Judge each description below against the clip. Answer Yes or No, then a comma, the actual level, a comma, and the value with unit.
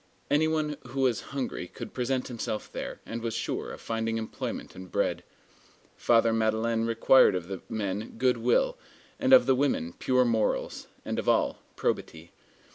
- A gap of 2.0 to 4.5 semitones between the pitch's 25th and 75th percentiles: Yes, average, 3.3 semitones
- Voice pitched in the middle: No, low, 115 Hz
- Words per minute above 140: Yes, average, 160 wpm